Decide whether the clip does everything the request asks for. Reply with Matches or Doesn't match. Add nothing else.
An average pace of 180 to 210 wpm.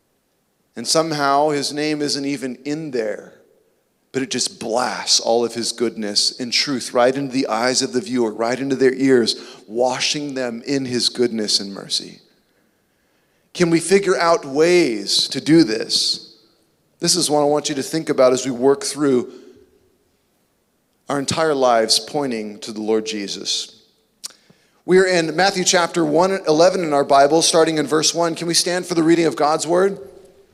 Doesn't match